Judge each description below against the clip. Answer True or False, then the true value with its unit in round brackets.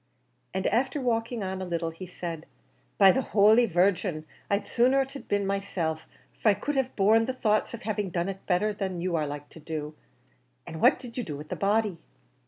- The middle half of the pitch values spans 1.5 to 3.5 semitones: False (4.7 semitones)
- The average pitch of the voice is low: False (195 Hz)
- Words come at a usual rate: False (210 wpm)